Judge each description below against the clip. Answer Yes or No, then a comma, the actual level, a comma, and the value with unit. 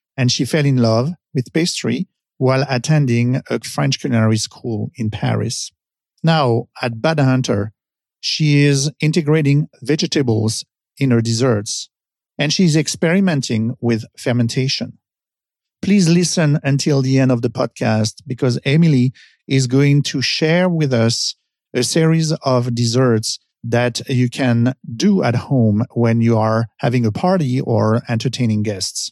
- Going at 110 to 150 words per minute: Yes, slow, 135 wpm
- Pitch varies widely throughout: No, average, 4.2 semitones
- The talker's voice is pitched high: No, low, 130 Hz